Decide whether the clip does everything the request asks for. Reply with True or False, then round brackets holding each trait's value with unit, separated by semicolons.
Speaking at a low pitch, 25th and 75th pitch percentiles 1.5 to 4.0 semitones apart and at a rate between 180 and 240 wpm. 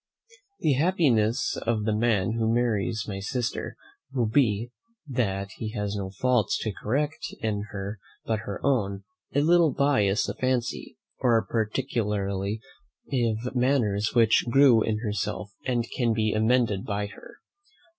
False (110 Hz; 3.4 semitones; 140 wpm)